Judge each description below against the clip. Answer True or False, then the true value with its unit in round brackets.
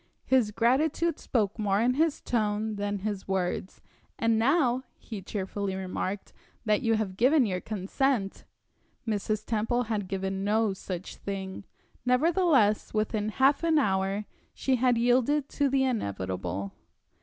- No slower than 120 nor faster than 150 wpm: True (140 wpm)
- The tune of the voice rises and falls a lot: False (4.5 semitones)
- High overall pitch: True (215 Hz)